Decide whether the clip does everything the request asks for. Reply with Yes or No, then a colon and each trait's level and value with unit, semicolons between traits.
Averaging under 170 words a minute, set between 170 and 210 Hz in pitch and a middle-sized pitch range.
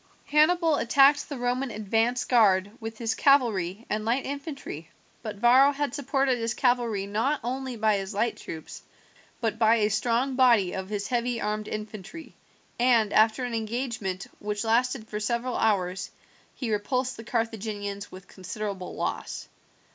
No: average, 150 wpm; high, 230 Hz; average, 3.3 semitones